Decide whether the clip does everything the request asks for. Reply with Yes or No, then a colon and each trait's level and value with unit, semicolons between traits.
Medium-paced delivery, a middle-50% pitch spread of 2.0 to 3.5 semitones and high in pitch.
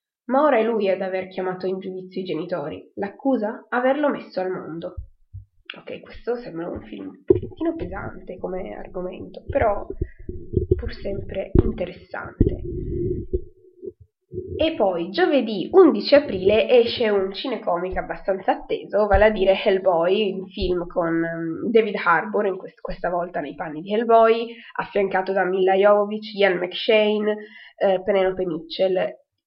No: average, 135 wpm; average, 4.1 semitones; high, 200 Hz